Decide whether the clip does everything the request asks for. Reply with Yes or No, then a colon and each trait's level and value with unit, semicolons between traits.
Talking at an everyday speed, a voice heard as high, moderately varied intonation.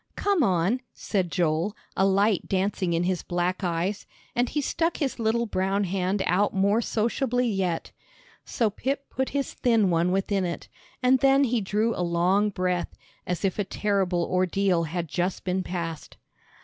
Yes: average, 165 wpm; high, 195 Hz; average, 4.0 semitones